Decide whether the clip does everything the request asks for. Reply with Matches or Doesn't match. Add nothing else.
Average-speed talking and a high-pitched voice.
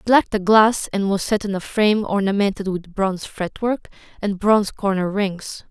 Matches